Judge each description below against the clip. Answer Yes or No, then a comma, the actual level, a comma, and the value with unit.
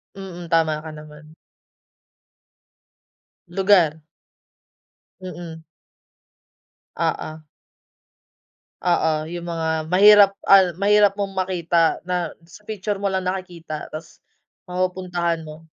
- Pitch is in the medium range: Yes, medium, 175 Hz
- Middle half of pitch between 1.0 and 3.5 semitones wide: Yes, average, 3.0 semitones